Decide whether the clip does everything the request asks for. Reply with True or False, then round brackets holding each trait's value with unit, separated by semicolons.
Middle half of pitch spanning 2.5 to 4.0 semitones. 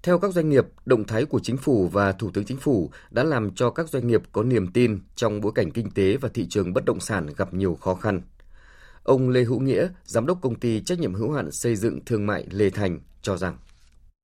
False (4.8 semitones)